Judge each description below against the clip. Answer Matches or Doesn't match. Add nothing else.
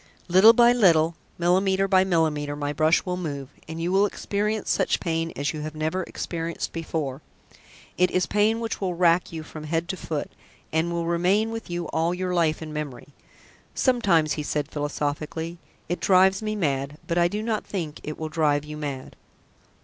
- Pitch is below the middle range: Doesn't match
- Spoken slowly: Doesn't match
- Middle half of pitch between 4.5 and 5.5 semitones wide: Doesn't match